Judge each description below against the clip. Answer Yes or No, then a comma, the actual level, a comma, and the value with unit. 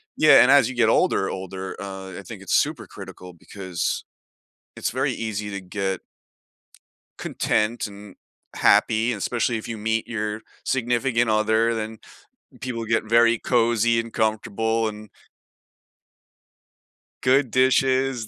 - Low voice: Yes, low, 110 Hz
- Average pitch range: No, narrow, 2.2 semitones